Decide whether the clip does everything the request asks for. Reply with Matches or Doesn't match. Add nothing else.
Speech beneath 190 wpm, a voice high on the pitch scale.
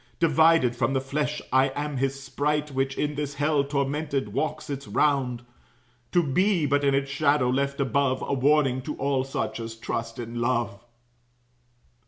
Doesn't match